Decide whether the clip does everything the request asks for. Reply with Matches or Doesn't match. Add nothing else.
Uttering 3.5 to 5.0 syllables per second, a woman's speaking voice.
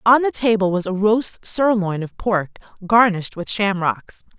Matches